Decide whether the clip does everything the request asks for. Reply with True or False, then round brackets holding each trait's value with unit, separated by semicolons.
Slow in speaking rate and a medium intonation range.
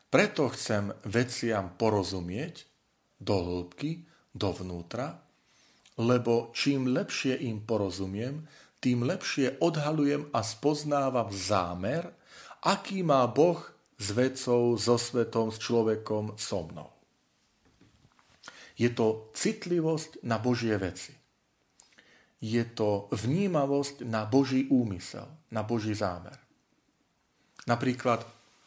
True (95 wpm; 4.3 semitones)